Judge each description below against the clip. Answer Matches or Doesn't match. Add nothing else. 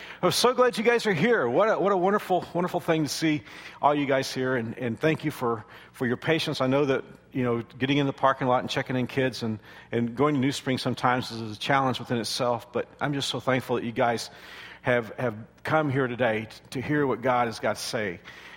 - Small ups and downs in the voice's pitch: Doesn't match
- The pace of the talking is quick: Matches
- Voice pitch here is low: Matches